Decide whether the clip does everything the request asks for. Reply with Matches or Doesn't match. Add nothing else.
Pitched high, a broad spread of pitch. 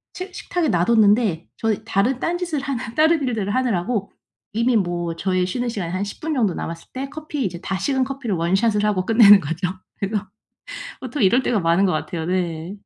Matches